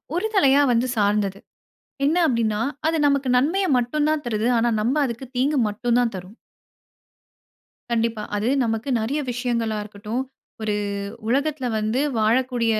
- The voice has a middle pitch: No, high, 235 Hz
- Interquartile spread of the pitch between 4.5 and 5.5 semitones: No, average, 3.8 semitones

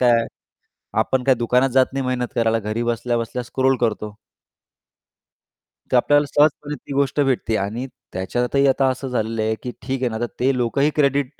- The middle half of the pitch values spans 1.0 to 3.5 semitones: Yes, average, 2.8 semitones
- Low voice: Yes, low, 125 Hz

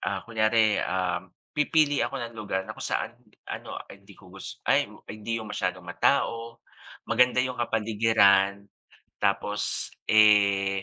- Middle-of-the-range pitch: No, low, 105 Hz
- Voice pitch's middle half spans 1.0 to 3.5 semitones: Yes, average, 2.8 semitones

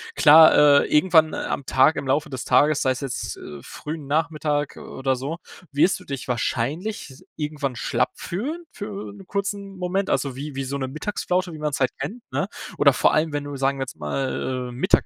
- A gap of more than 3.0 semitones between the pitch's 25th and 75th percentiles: Yes, average, 4.3 semitones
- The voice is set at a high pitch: No, medium, 150 Hz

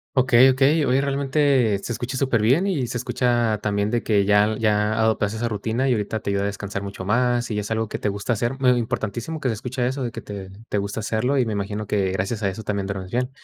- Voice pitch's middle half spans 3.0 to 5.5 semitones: Yes, average, 3.5 semitones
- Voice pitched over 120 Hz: No, low, 110 Hz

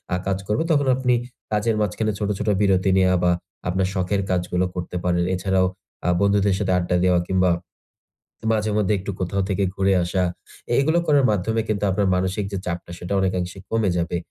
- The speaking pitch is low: Yes, very low, 95 Hz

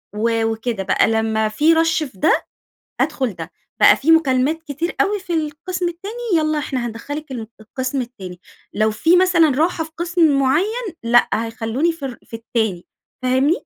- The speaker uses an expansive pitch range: Yes, wide, 6.2 semitones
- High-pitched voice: Yes, very high, 275 Hz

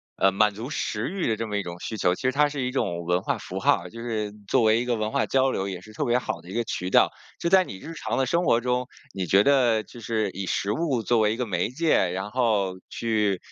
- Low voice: Yes, low, 110 Hz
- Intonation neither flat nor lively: Yes, average, 4.2 semitones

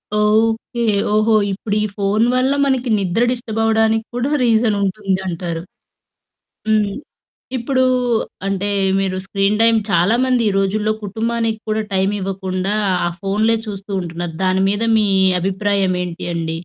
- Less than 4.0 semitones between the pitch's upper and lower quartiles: Yes, average, 2.8 semitones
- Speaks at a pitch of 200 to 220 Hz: Yes, high, 210 Hz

